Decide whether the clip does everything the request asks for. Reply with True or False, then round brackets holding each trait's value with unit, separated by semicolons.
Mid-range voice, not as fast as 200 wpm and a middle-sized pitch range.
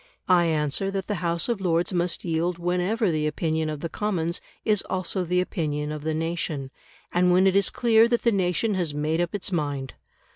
False (175 Hz; 205 wpm; 3.3 semitones)